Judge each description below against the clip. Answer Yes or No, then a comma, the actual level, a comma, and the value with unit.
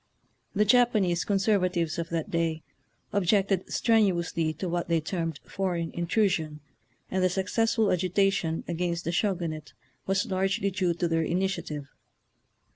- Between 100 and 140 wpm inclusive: Yes, slow, 135 wpm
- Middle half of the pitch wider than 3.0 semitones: No, average, 2.7 semitones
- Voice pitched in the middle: Yes, medium, 180 Hz